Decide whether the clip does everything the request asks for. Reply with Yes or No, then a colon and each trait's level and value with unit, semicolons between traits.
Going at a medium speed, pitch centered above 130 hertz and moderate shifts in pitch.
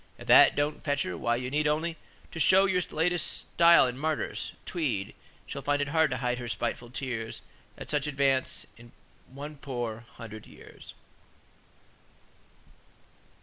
Yes: average, 150 wpm; medium, 140 Hz; average, 4.1 semitones